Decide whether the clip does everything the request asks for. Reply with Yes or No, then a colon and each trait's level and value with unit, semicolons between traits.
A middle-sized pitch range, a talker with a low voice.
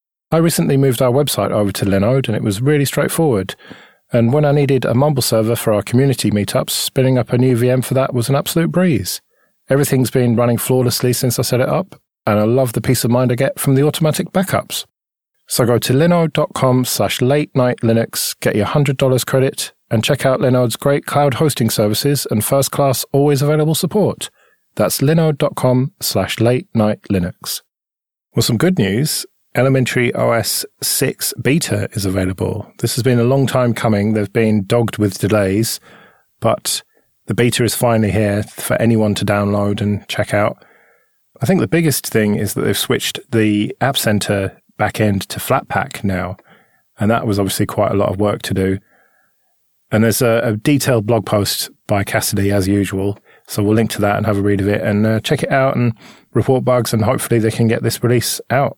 Yes: average, 4.2 semitones; low, 120 Hz